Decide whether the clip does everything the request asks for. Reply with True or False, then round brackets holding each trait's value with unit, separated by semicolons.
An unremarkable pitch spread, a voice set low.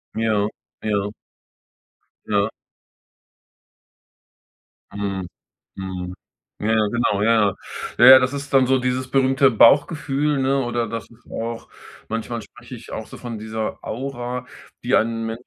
True (3.3 semitones; 115 Hz)